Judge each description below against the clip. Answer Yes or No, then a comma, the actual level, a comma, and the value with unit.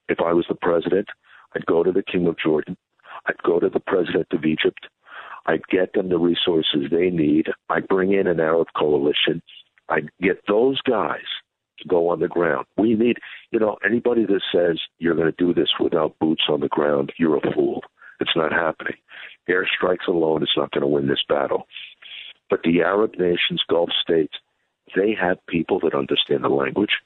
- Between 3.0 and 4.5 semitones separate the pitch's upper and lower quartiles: Yes, average, 3.9 semitones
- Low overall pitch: Yes, very low, 85 Hz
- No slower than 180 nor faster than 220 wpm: Yes, average, 190 wpm